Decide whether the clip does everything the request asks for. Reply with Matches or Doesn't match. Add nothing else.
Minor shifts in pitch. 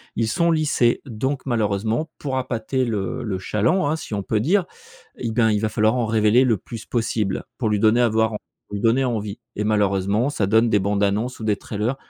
Doesn't match